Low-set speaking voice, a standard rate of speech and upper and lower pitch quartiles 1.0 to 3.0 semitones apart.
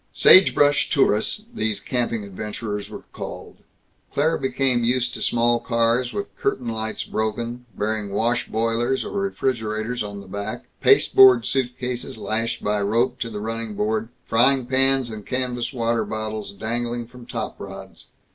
Yes: low, 115 Hz; average, 145 wpm; average, 2.7 semitones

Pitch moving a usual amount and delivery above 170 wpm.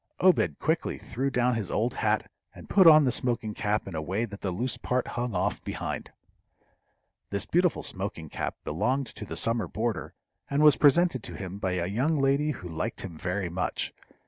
No: wide, 6.1 semitones; average, 195 wpm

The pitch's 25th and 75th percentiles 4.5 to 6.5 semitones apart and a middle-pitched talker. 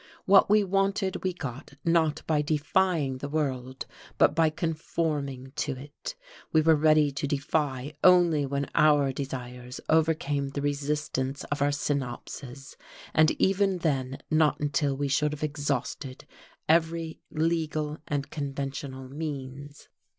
No: narrow, 2.5 semitones; medium, 145 Hz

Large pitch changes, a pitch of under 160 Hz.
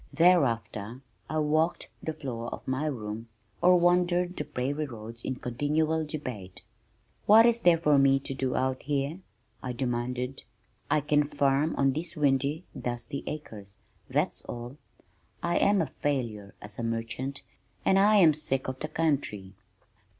No: average, 4.4 semitones; medium, 140 Hz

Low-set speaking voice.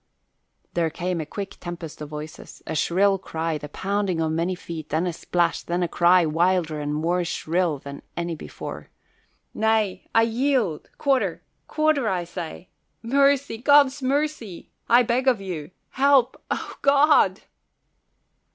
No: medium, 185 Hz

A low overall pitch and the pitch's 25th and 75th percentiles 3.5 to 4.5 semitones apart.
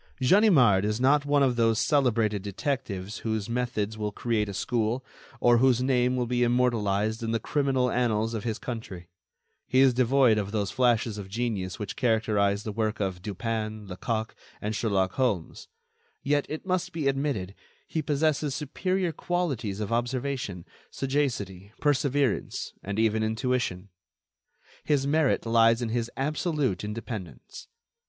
Yes: low, 115 Hz; average, 4.1 semitones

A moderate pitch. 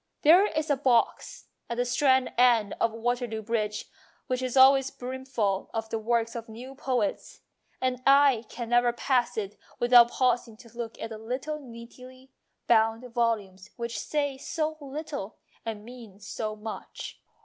No: high, 240 Hz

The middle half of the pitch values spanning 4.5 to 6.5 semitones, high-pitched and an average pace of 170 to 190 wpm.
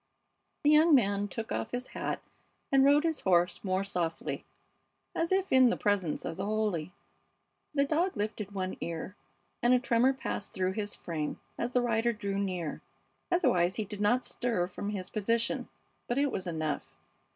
Yes: average, 5.1 semitones; high, 210 Hz; average, 175 wpm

